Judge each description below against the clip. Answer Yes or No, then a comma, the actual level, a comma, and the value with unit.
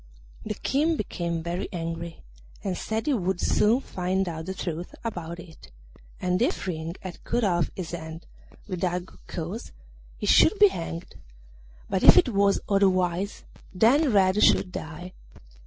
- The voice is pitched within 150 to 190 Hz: Yes, medium, 185 Hz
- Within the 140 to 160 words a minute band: Yes, average, 155 wpm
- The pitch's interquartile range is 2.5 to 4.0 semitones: Yes, average, 3.3 semitones